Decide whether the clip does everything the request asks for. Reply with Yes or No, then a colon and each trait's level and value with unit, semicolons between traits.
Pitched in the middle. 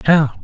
Yes: medium, 145 Hz